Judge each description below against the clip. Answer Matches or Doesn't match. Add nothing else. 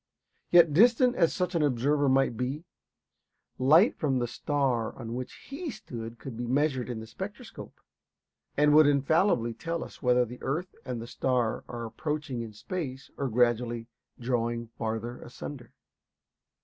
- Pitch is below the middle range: Matches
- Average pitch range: Matches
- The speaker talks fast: Doesn't match